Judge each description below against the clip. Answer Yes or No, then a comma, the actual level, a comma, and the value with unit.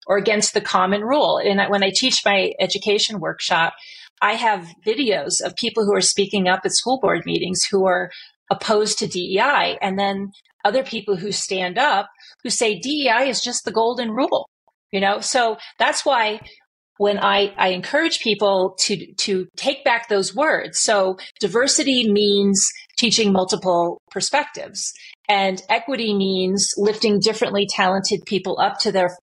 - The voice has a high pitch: Yes, high, 205 Hz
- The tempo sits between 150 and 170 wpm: Yes, average, 160 wpm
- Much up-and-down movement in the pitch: No, average, 2.8 semitones